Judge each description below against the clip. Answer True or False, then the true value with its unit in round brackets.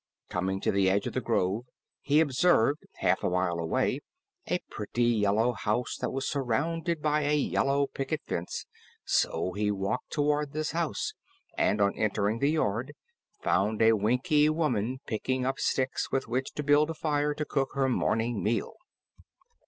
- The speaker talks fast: False (165 wpm)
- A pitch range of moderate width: False (5.8 semitones)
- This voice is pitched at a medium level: False (130 Hz)